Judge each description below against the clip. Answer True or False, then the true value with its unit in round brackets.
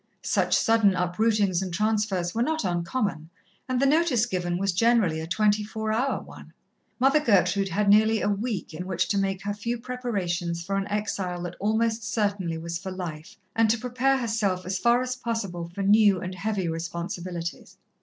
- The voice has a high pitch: True (200 Hz)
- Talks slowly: False (180 wpm)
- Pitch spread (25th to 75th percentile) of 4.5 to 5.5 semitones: False (4.1 semitones)